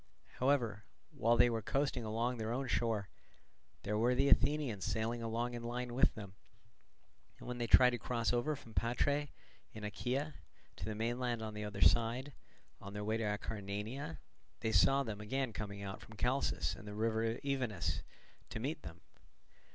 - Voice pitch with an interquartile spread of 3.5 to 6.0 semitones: No, average, 2.9 semitones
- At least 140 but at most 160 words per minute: No, average, 175 wpm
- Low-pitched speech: Yes, low, 115 Hz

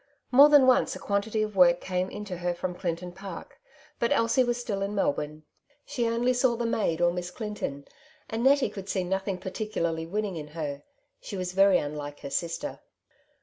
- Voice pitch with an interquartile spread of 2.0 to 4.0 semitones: No, average, 4.8 semitones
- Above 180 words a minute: Yes, average, 190 wpm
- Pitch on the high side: Yes, high, 195 Hz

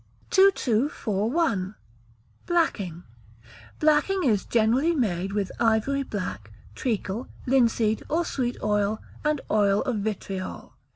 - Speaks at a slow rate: Yes, slow, 100 wpm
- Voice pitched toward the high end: Yes, high, 220 Hz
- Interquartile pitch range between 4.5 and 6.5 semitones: Yes, wide, 5.6 semitones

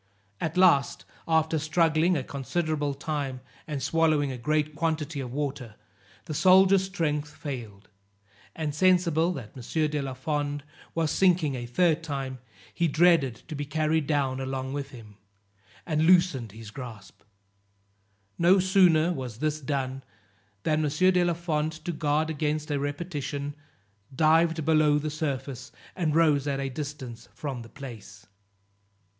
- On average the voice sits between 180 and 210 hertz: No, medium, 150 Hz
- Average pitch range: Yes, average, 3.1 semitones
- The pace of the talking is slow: No, average, 145 wpm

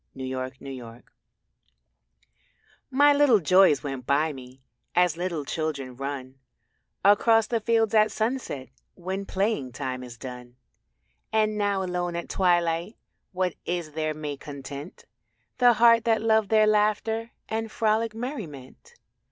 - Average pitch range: No, wide, 7.8 semitones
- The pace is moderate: No, slow, 130 wpm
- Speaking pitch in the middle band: Yes, medium, 180 Hz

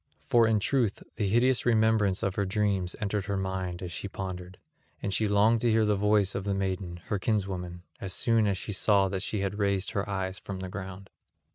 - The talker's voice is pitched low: Yes, low, 100 Hz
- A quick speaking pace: Yes, fast, 215 wpm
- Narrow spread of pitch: Yes, narrow, 2.0 semitones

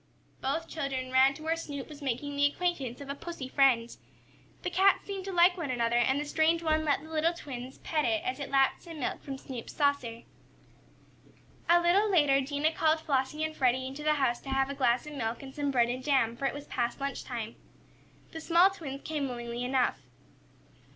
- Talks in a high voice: Yes, very high, 280 Hz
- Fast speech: Yes, fast, 210 wpm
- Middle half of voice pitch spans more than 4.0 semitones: No, average, 3.4 semitones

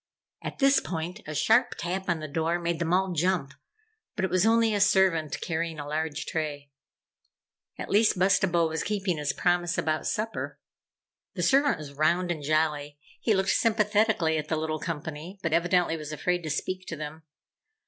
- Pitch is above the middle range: No, medium, 170 Hz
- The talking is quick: No, average, 180 wpm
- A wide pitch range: No, average, 3.5 semitones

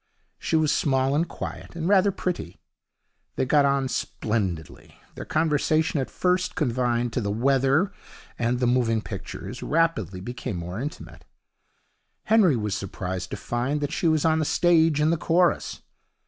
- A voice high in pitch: No, medium, 140 Hz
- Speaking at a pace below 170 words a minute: Yes, average, 155 wpm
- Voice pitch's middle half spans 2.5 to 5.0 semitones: No, wide, 5.5 semitones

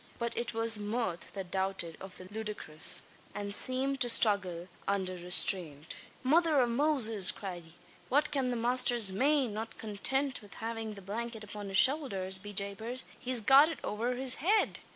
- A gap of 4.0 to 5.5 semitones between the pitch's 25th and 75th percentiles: Yes, average, 4.7 semitones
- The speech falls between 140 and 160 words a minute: No, average, 170 wpm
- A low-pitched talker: No, high, 220 Hz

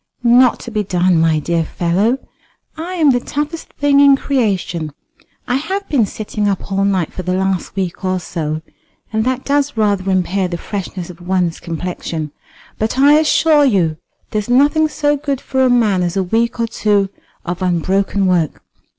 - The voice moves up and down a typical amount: No, wide, 6.6 semitones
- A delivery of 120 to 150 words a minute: No, average, 175 wpm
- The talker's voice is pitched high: Yes, high, 200 Hz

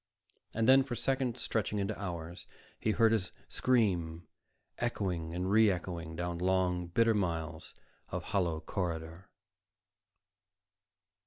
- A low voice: Yes, very low, 95 Hz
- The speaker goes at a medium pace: No, slow, 115 wpm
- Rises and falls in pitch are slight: No, average, 4.5 semitones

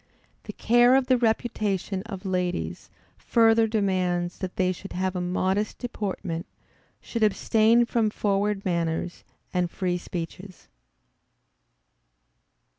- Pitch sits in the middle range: No, high, 195 Hz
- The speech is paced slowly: Yes, slow, 115 wpm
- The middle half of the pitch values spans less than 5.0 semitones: Yes, average, 3.6 semitones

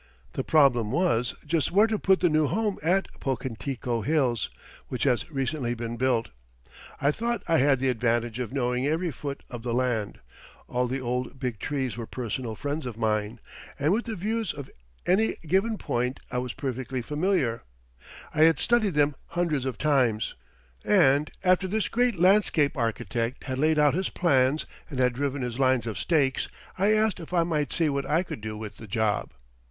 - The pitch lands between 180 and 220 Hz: No, low, 135 Hz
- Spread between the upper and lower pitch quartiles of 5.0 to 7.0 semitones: Yes, wide, 5.4 semitones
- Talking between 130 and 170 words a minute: No, average, 185 wpm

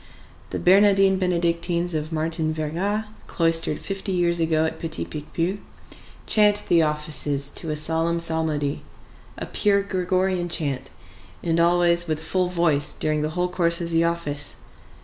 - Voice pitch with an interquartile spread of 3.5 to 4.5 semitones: No, narrow, 2.4 semitones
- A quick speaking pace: No, average, 145 wpm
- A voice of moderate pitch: Yes, medium, 170 Hz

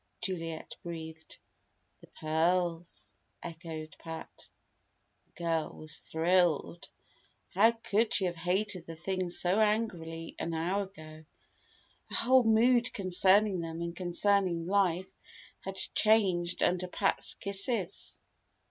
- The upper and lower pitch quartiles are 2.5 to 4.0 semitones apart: Yes, average, 3.3 semitones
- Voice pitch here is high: No, medium, 180 Hz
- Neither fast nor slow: No, slow, 110 wpm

